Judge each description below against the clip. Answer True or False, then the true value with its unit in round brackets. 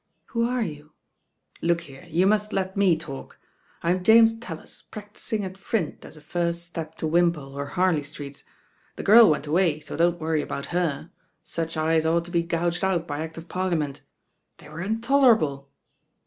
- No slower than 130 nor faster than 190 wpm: True (175 wpm)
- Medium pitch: True (170 Hz)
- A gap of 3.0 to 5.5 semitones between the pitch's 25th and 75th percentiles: True (3.4 semitones)